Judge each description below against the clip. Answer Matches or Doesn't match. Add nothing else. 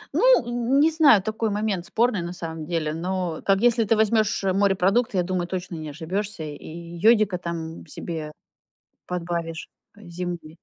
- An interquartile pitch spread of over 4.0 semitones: Matches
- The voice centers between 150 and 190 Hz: Matches